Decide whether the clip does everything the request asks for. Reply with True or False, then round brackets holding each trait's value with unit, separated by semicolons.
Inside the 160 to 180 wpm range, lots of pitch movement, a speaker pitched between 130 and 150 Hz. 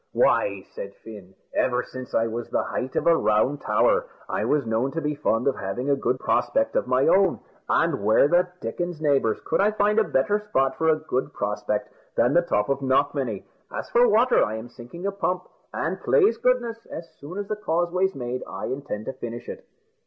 False (205 wpm; 7.2 semitones; 140 Hz)